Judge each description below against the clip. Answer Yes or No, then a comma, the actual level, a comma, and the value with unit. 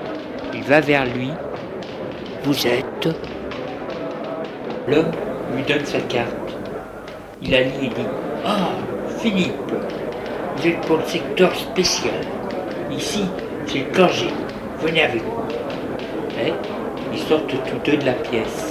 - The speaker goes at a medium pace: No, slow, 125 wpm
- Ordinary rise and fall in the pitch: Yes, average, 4.2 semitones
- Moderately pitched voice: Yes, medium, 145 Hz